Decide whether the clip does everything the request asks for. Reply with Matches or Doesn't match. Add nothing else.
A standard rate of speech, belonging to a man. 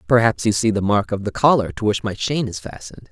Doesn't match